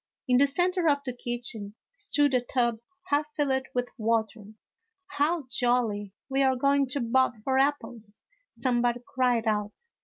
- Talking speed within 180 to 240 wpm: No, average, 165 wpm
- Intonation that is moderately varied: Yes, average, 3.2 semitones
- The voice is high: Yes, very high, 255 Hz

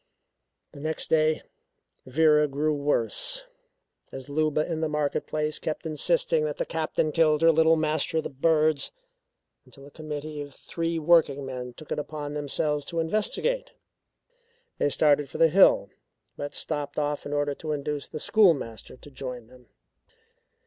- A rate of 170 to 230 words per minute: No, average, 155 wpm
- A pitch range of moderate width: No, narrow, 2.0 semitones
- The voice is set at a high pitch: No, medium, 150 Hz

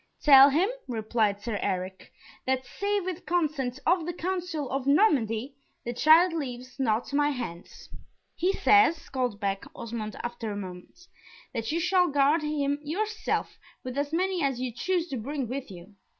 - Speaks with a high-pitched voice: Yes, very high, 275 Hz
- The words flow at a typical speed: Yes, average, 165 wpm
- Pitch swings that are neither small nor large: No, wide, 6.2 semitones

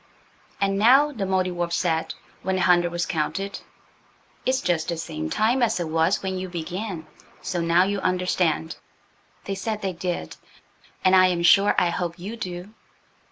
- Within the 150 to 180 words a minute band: Yes, average, 165 wpm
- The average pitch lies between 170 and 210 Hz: Yes, medium, 185 Hz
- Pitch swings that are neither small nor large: No, narrow, 2.3 semitones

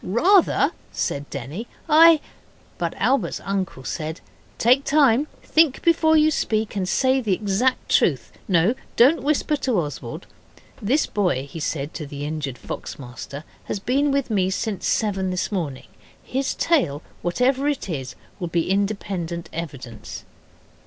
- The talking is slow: No, average, 145 wpm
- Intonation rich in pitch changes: Yes, wide, 9.0 semitones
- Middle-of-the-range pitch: No, high, 195 Hz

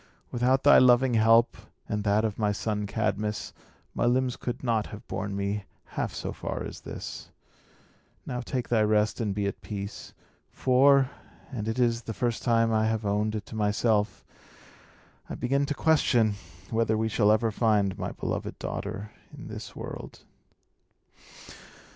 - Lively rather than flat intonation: No, narrow, 2.6 semitones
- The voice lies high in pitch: No, low, 110 Hz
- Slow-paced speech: No, average, 160 wpm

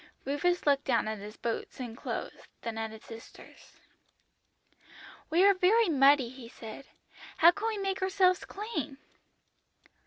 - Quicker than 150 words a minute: No, average, 145 wpm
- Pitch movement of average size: No, wide, 8.4 semitones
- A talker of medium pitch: No, very high, 285 Hz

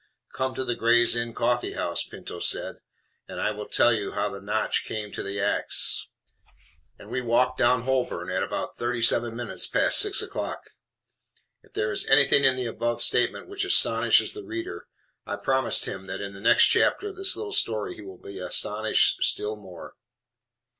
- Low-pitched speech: Yes, low, 120 Hz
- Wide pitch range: No, average, 3.6 semitones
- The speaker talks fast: No, average, 185 wpm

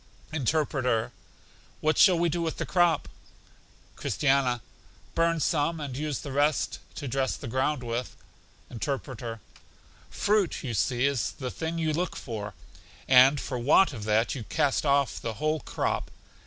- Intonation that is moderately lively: Yes, average, 4.0 semitones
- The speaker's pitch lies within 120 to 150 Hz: Yes, medium, 140 Hz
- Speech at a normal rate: Yes, average, 150 wpm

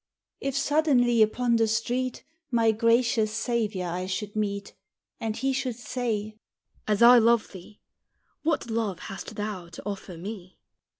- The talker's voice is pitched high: Yes, high, 225 Hz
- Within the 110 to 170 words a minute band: Yes, average, 140 wpm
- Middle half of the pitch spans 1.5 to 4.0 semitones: Yes, average, 2.8 semitones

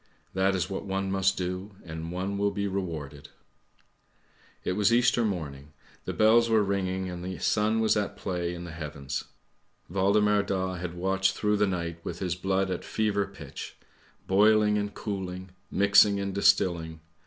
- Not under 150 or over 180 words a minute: Yes, average, 170 wpm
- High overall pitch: No, very low, 95 Hz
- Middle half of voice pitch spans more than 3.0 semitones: No, narrow, 2.5 semitones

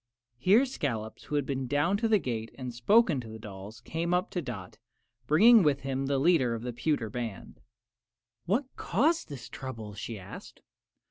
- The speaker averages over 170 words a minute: Yes, average, 180 wpm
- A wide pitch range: Yes, wide, 7.5 semitones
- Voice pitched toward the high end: No, low, 135 Hz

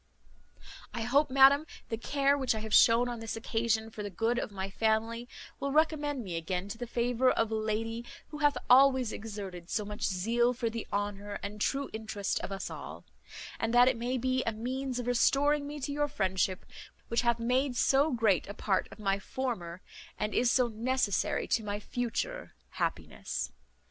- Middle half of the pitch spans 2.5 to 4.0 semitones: Yes, average, 3.6 semitones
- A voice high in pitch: Yes, high, 230 Hz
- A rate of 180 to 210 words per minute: Yes, average, 190 wpm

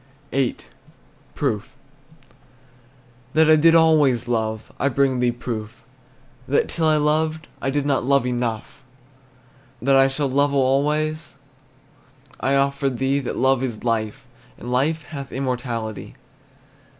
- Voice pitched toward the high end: No, low, 135 Hz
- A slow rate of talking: Yes, slow, 125 wpm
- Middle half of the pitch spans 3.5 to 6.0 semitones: No, average, 3.0 semitones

